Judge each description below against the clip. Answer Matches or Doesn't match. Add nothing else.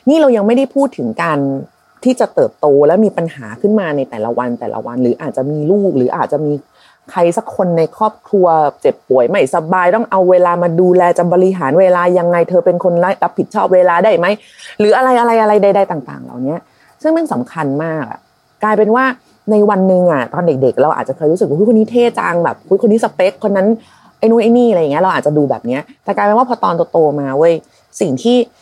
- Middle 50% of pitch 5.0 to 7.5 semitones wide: Matches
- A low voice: Doesn't match